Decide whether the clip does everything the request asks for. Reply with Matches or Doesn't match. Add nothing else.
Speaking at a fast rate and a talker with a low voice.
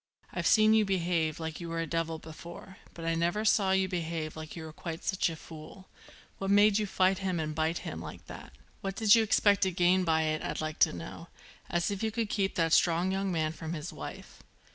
Doesn't match